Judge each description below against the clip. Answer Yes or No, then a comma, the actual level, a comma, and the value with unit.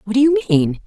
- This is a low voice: No, high, 215 Hz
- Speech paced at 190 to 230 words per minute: No, fast, 280 wpm